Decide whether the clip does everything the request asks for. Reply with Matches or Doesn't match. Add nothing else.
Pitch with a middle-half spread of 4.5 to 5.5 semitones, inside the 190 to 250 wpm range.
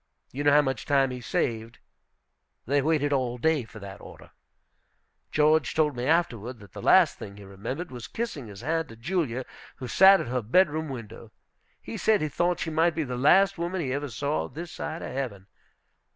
Matches